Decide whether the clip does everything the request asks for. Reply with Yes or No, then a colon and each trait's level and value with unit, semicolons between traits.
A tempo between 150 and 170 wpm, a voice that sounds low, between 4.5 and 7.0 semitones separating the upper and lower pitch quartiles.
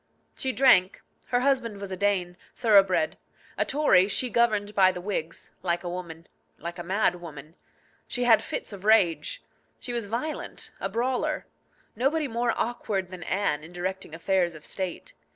No: average, 165 wpm; high, 200 Hz; average, 5.1 semitones